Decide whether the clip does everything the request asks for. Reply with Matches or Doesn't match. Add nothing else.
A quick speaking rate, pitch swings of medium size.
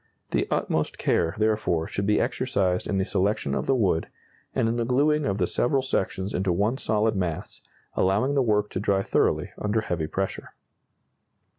Doesn't match